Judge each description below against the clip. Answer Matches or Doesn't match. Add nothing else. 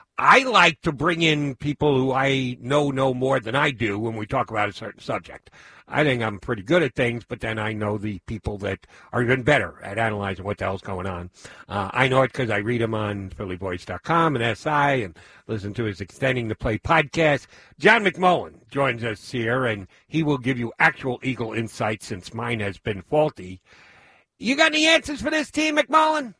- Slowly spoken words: Doesn't match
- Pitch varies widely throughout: Matches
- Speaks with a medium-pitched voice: Doesn't match